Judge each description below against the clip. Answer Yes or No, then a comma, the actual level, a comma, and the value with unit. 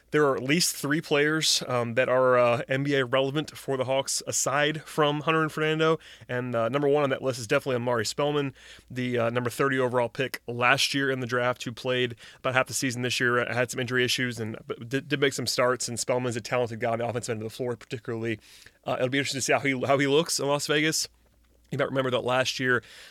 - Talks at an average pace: No, fast, 240 wpm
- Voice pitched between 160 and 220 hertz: No, low, 130 Hz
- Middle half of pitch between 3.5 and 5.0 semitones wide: No, narrow, 2.5 semitones